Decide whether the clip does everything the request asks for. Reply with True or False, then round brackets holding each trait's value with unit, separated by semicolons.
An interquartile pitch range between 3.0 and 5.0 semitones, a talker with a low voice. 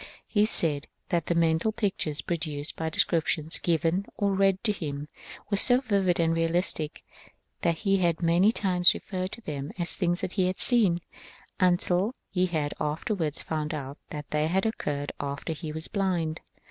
False (3.5 semitones; 170 Hz)